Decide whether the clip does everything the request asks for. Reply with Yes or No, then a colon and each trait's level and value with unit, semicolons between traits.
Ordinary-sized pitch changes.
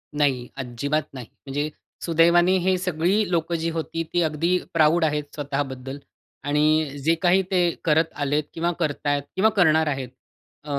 Yes: average, 3.0 semitones